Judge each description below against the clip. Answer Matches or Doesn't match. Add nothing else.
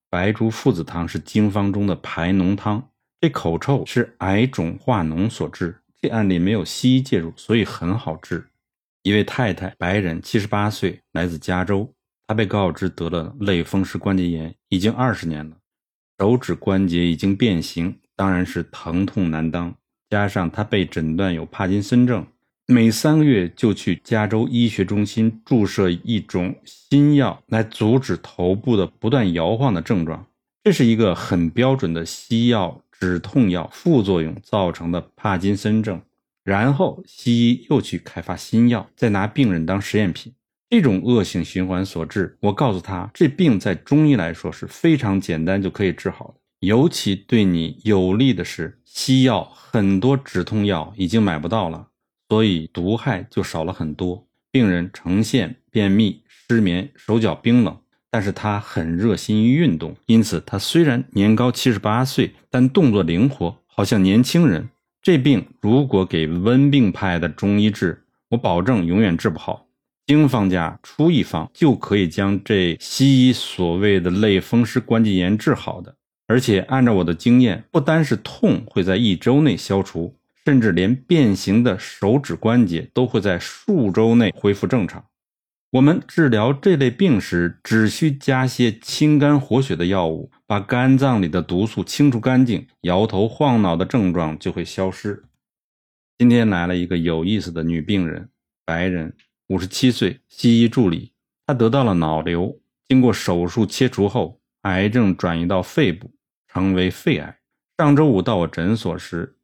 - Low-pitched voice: Matches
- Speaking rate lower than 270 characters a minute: Matches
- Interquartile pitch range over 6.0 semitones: Doesn't match